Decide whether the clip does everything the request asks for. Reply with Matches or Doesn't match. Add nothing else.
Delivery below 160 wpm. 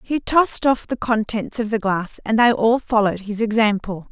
Doesn't match